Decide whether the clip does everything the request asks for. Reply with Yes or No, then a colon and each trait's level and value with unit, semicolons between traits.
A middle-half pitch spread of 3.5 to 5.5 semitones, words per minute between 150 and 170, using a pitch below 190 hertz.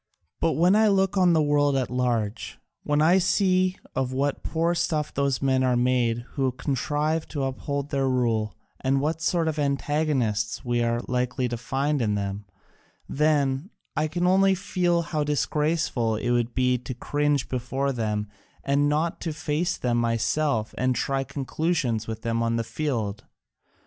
Yes: average, 4.3 semitones; average, 165 wpm; low, 135 Hz